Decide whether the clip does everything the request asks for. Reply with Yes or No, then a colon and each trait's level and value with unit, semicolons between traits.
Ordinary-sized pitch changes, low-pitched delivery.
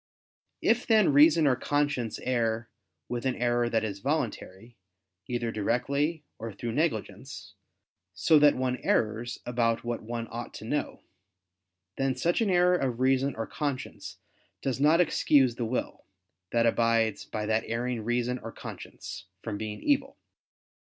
Yes: average, 4.1 semitones; low, 120 Hz